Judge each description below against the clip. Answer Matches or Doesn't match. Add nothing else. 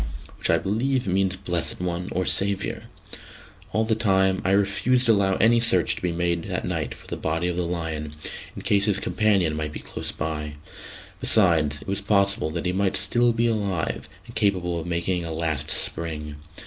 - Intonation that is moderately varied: Matches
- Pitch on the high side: Doesn't match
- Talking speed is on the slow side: Doesn't match